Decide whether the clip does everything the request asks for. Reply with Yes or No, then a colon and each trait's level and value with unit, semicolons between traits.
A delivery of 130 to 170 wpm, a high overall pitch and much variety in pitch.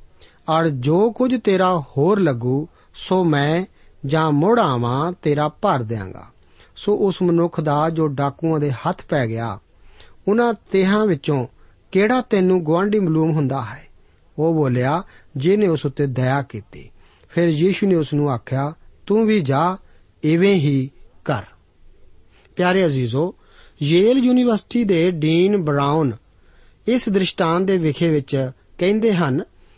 No: average, 135 wpm; medium, 155 Hz; wide, 6.4 semitones